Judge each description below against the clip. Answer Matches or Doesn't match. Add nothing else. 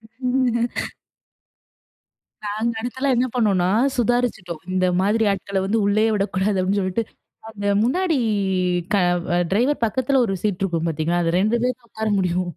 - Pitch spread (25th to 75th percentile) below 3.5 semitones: Doesn't match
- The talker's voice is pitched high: Matches